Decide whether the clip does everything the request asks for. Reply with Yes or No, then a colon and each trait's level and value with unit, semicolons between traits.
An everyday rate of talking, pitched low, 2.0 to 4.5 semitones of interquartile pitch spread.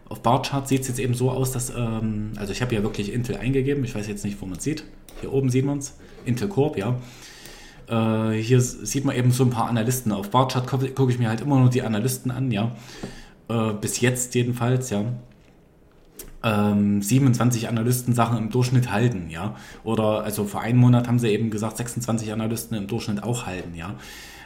No: fast, 205 wpm; low, 120 Hz; average, 2.9 semitones